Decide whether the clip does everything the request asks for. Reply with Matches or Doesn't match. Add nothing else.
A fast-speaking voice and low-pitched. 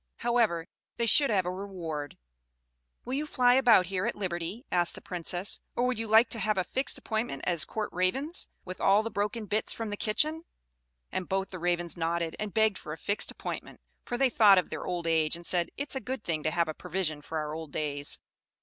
Doesn't match